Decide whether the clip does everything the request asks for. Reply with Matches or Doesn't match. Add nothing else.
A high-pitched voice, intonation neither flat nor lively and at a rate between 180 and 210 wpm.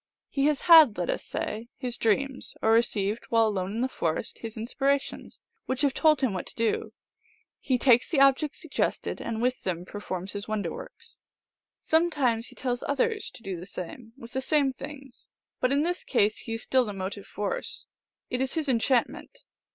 Matches